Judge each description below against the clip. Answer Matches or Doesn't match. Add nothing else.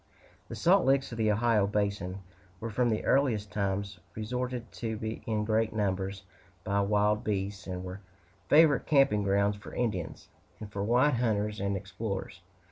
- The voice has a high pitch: Doesn't match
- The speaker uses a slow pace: Doesn't match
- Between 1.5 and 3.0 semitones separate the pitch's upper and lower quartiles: Matches